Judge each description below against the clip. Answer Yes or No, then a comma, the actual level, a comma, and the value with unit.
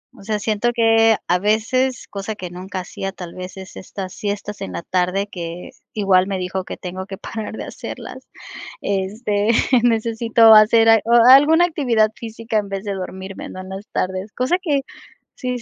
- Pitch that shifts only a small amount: No, average, 3.1 semitones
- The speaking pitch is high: Yes, high, 205 Hz